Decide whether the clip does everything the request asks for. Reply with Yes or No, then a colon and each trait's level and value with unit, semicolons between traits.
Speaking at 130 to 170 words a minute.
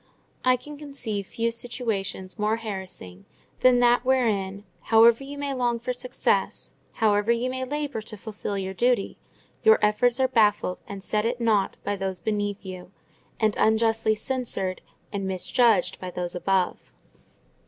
Yes: average, 150 wpm